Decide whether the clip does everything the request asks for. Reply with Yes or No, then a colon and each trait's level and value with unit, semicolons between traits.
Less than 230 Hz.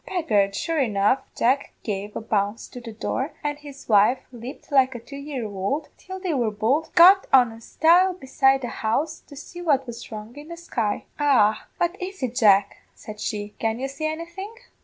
No: very high, 265 Hz